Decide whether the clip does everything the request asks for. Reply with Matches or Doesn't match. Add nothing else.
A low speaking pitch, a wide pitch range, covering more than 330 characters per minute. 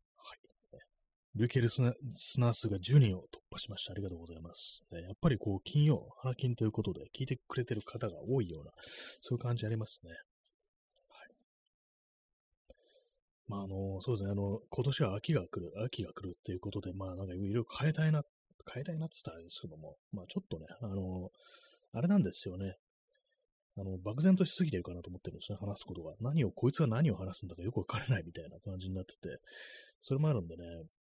Matches